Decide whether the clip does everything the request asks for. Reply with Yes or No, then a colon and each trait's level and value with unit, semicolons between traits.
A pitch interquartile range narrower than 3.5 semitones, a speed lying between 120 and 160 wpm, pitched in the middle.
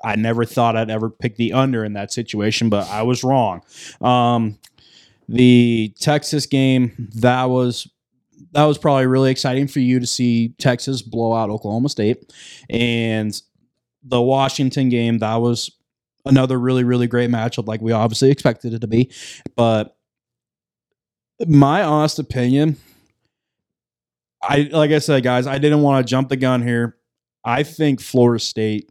No: average, 2.8 semitones; average, 155 wpm; low, 125 Hz